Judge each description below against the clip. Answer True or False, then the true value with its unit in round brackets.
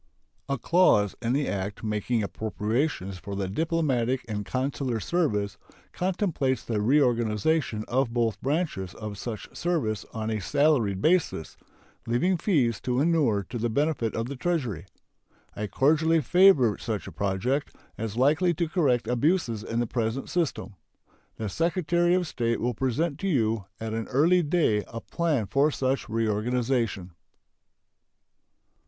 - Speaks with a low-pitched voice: True (125 Hz)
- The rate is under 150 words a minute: True (140 wpm)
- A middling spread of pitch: False (6.2 semitones)